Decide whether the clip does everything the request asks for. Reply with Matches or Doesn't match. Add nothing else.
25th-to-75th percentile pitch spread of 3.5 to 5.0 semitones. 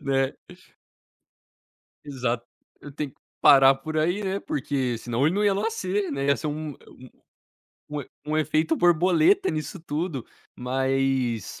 Matches